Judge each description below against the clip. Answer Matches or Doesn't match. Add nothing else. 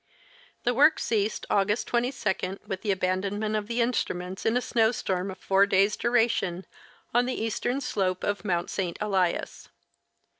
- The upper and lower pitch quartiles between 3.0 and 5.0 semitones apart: Matches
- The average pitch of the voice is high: Matches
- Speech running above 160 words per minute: Doesn't match